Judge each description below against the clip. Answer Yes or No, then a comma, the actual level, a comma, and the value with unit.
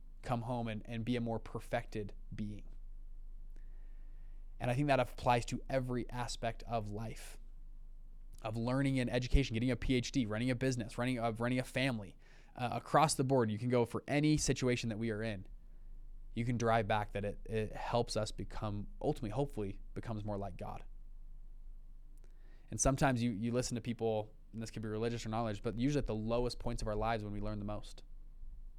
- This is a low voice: Yes, low, 115 Hz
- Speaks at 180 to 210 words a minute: Yes, average, 190 wpm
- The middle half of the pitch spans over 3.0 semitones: No, narrow, 2.6 semitones